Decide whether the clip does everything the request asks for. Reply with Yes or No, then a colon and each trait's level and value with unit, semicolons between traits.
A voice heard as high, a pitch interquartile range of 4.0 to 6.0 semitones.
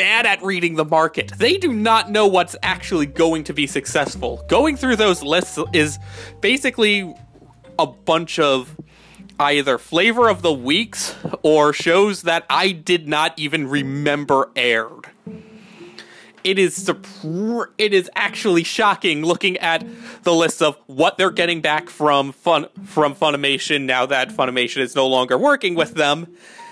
No: medium, 165 Hz; average, 5.3 semitones